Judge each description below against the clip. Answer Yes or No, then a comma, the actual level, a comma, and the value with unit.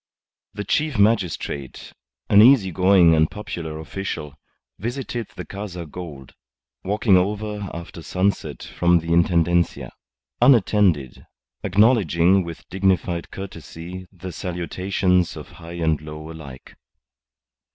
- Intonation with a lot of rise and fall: No, average, 3.4 semitones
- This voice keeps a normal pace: No, slow, 110 wpm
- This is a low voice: Yes, very low, 90 Hz